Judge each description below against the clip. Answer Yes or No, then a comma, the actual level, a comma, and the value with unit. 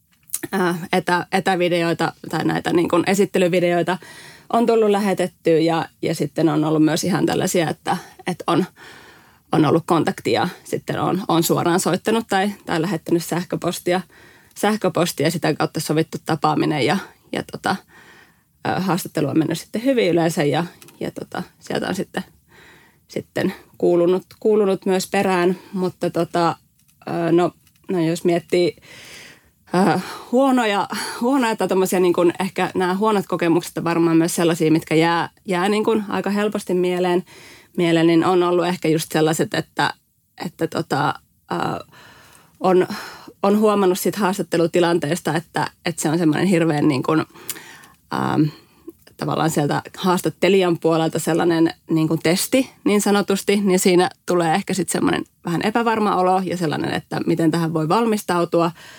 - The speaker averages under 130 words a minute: No, average, 135 wpm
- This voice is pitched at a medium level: Yes, medium, 175 Hz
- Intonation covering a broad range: No, narrow, 2.4 semitones